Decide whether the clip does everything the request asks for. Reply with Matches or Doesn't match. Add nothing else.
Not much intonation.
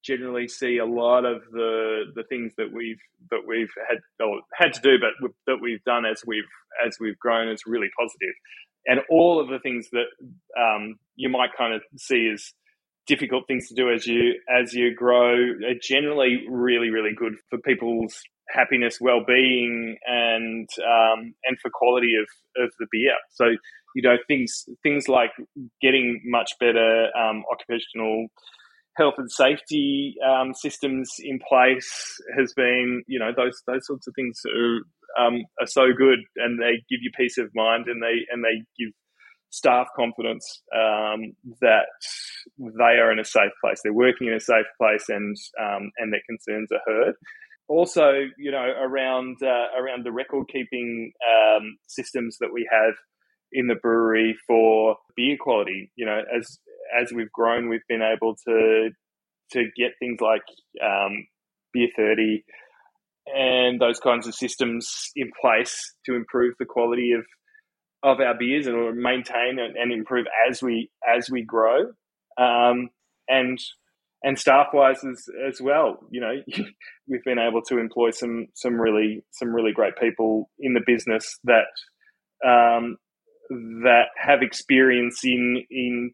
Matches